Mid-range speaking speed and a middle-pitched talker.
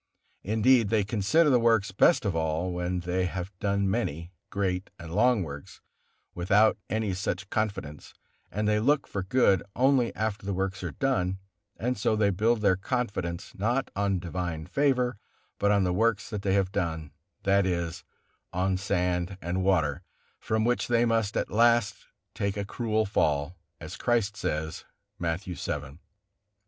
No: average, 155 wpm; low, 100 Hz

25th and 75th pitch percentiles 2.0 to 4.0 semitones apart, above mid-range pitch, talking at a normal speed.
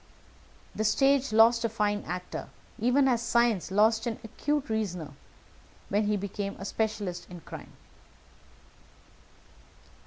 No: average, 2.8 semitones; high, 220 Hz; slow, 120 wpm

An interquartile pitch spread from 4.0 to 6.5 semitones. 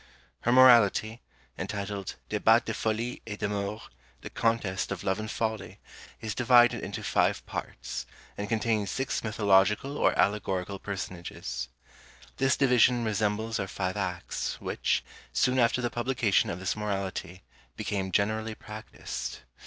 No: average, 3.0 semitones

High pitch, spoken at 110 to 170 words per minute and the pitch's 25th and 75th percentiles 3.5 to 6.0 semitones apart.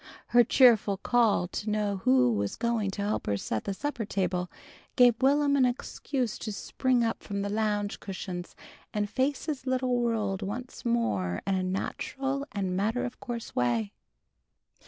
Yes: high, 215 Hz; average, 165 wpm; average, 4.5 semitones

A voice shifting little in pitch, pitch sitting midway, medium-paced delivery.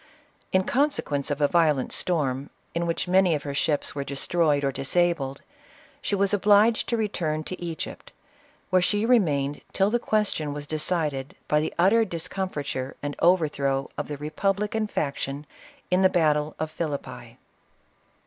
No: average, 4.8 semitones; medium, 160 Hz; average, 155 wpm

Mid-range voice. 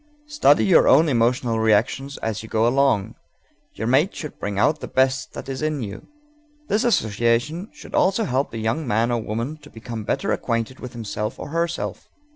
No: low, 125 Hz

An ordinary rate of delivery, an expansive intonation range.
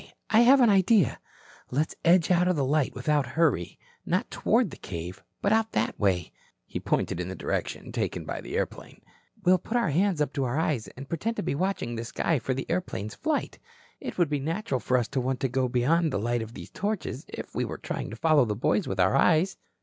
No: fast, 225 wpm; wide, 7.1 semitones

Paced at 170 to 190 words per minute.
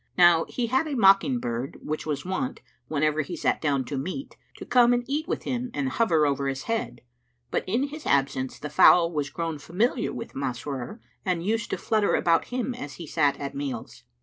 No: average, 200 wpm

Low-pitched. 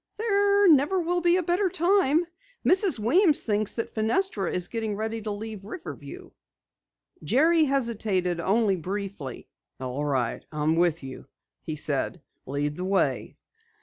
No: high, 220 Hz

